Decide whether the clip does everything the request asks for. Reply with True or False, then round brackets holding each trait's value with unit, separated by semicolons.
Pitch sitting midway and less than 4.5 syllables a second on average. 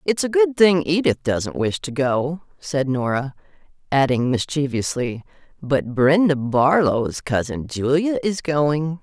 True (150 Hz; 3.9 syllables/s)